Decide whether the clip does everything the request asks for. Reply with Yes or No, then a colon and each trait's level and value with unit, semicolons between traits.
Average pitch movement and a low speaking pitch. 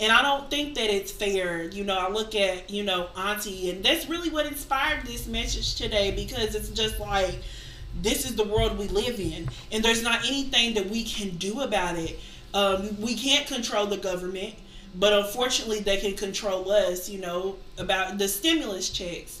No: average, 3.5 semitones; high, 205 Hz